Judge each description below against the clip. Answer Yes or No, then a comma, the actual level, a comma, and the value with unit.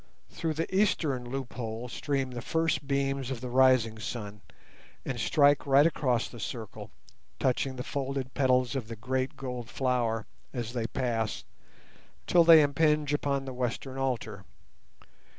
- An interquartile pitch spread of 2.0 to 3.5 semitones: Yes, narrow, 2.5 semitones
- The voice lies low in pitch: Yes, low, 130 Hz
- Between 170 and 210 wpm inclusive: No, average, 145 wpm